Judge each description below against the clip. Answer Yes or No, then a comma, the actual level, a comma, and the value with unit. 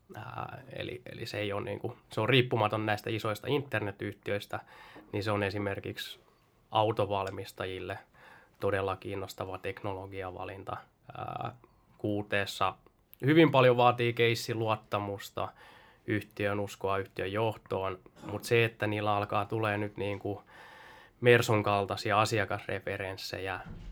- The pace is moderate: Yes, average, 110 wpm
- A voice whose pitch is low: Yes, low, 105 Hz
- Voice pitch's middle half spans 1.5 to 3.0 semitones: Yes, average, 2.7 semitones